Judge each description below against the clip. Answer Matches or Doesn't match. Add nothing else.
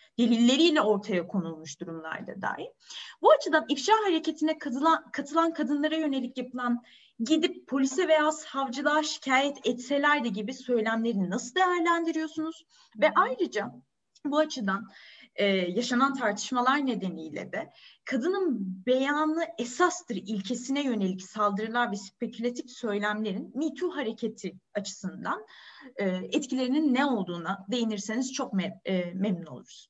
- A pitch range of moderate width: Doesn't match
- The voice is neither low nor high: Doesn't match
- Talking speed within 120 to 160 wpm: Doesn't match